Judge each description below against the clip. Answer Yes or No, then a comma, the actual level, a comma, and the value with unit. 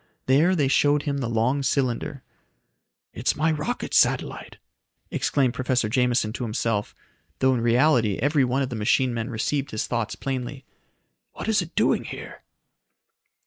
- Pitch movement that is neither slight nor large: Yes, average, 3.3 semitones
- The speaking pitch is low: Yes, low, 130 Hz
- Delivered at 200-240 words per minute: No, average, 150 wpm